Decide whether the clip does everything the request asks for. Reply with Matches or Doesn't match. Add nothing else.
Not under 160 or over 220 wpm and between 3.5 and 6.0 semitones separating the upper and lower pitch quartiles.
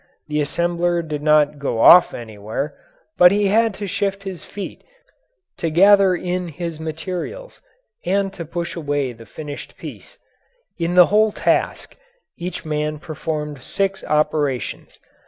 Doesn't match